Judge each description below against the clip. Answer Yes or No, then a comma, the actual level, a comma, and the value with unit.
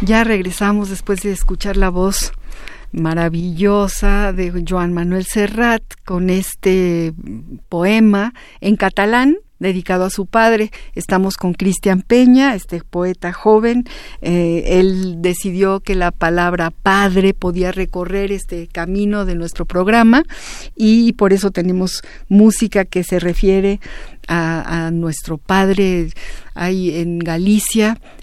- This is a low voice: No, high, 190 Hz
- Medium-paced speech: No, slow, 120 wpm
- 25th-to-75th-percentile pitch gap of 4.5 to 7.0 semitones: No, narrow, 2.5 semitones